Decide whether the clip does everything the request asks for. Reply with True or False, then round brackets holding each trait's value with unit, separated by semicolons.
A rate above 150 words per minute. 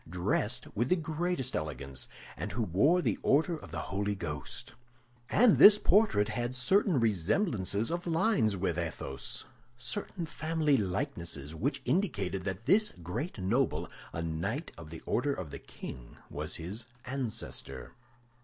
False (145 wpm)